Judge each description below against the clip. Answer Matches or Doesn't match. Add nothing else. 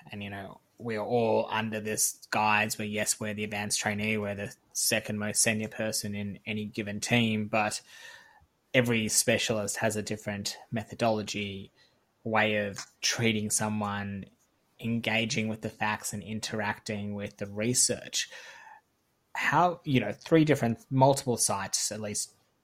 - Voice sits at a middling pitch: Doesn't match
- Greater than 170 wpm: Doesn't match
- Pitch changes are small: Matches